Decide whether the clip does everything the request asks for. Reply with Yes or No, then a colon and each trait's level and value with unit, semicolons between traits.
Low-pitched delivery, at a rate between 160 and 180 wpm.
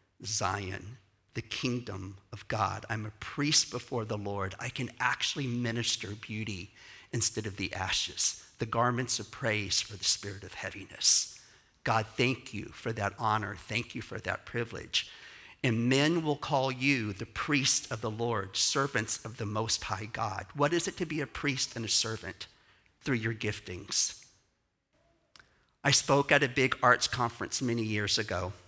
Yes: low, 115 Hz; average, 165 wpm